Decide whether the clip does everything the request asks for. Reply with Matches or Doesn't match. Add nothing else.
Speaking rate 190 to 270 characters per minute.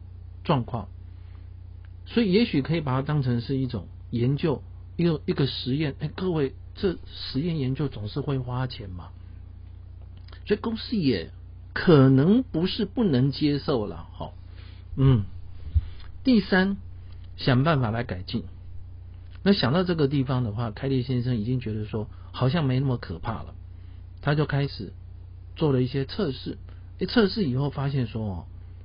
Matches